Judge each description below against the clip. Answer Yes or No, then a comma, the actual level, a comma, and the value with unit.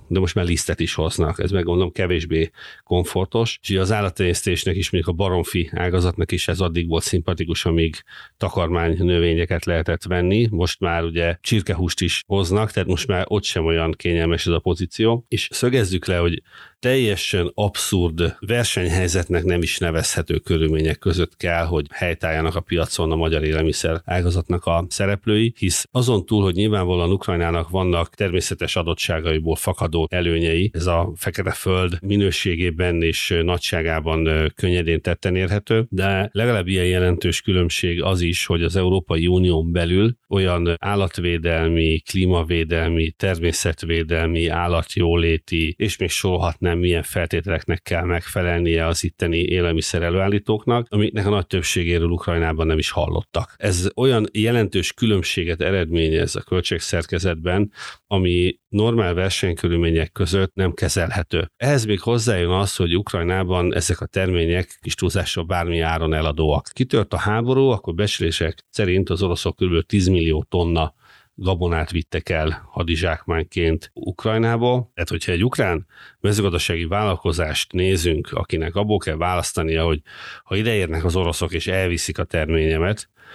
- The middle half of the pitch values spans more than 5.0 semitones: No, average, 2.7 semitones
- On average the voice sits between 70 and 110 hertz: Yes, very low, 90 Hz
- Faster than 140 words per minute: No, average, 135 wpm